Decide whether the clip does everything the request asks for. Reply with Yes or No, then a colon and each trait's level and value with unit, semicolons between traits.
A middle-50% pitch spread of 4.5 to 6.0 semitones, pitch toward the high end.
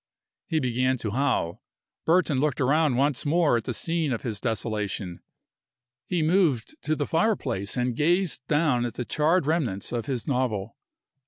No: average, 4.9 semitones; low, 130 Hz